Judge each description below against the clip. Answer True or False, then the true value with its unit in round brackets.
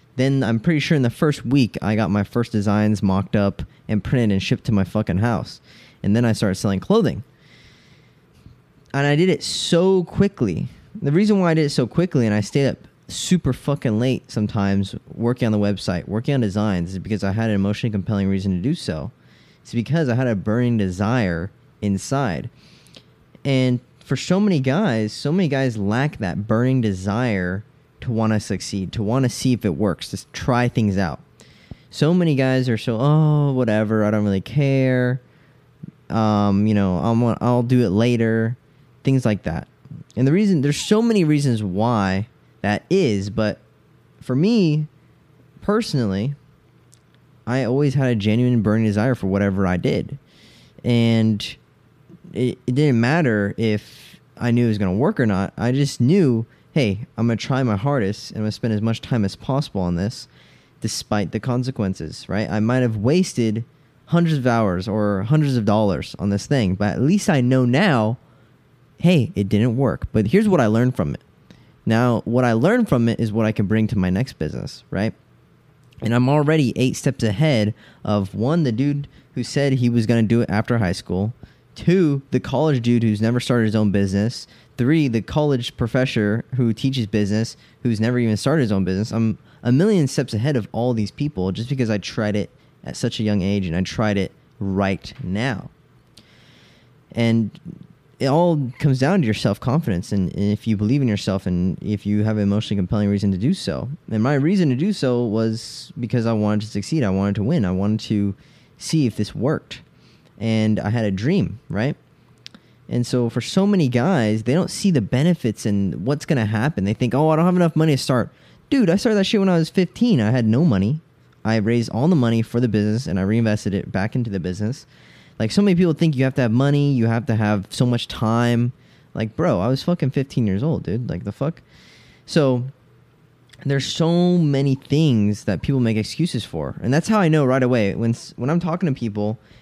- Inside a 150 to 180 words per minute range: False (200 wpm)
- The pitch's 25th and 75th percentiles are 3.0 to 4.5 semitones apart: False (4.9 semitones)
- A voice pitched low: True (120 Hz)